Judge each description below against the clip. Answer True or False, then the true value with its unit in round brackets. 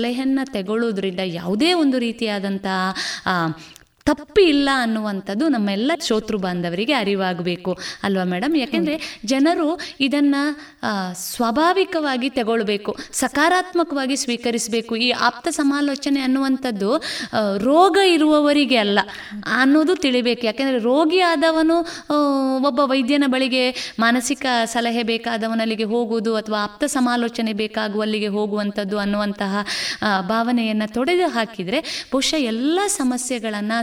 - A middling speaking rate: True (95 wpm)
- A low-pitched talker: False (245 Hz)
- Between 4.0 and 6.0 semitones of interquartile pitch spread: True (5.2 semitones)